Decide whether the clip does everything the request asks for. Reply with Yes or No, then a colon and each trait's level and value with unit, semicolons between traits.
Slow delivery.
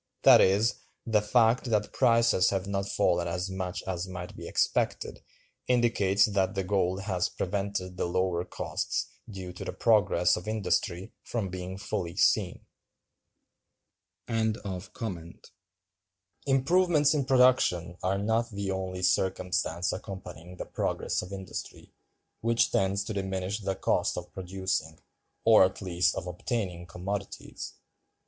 Yes: slow, 130 wpm